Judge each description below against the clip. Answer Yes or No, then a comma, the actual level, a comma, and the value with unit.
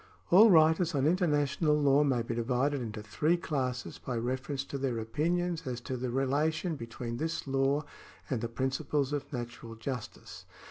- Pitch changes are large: No, average, 3.8 semitones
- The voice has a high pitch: No, low, 135 Hz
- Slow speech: No, average, 165 wpm